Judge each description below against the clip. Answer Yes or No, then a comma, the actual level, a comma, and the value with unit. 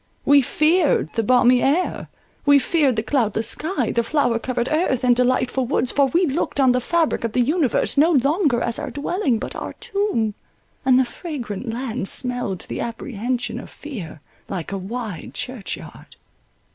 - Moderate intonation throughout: Yes, average, 3.8 semitones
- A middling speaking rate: Yes, average, 170 wpm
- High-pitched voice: Yes, very high, 255 Hz